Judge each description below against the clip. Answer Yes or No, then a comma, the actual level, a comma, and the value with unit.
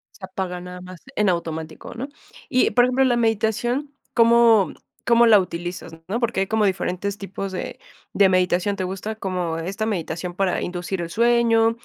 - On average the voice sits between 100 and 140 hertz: No, high, 195 Hz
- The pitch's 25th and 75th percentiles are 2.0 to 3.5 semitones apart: No, average, 4.1 semitones